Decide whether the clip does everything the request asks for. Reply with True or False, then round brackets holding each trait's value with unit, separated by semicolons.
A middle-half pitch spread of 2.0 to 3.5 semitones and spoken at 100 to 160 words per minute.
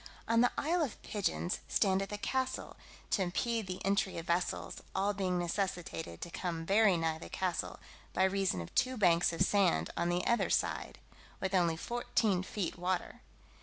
False (3.0 semitones; 170 wpm)